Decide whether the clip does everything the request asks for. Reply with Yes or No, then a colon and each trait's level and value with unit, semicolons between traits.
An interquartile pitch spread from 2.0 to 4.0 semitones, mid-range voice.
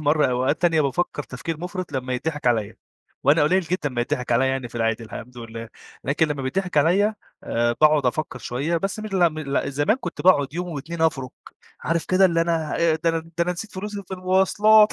No: average, 5.2 semitones; medium, 155 Hz